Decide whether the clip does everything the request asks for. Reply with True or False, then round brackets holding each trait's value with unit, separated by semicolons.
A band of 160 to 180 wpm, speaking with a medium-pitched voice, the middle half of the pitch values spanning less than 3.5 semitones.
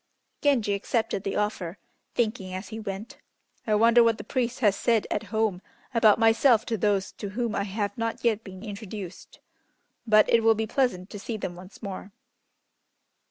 False (175 wpm; 215 Hz; 2.4 semitones)